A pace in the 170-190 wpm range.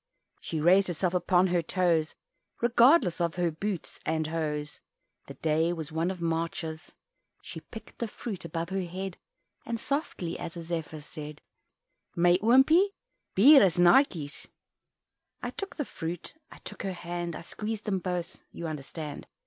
No: average, 155 wpm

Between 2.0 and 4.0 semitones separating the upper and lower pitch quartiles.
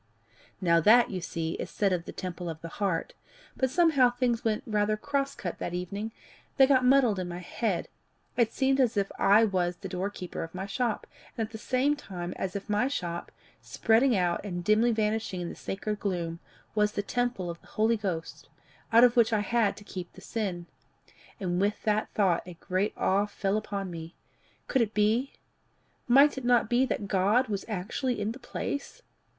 No: average, 4.6 semitones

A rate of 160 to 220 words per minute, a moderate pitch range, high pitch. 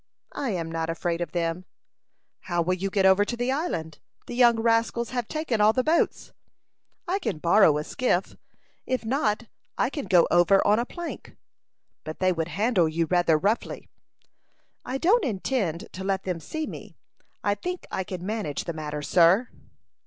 No: average, 175 wpm; wide, 6.2 semitones; high, 195 Hz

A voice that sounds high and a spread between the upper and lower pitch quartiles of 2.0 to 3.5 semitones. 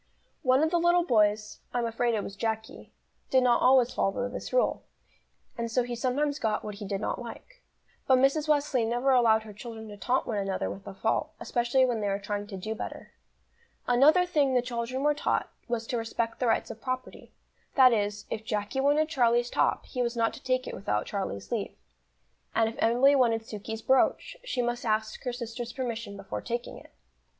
Yes: high, 235 Hz; average, 2.9 semitones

